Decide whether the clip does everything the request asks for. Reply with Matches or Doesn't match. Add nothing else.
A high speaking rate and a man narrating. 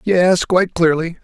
Doesn't match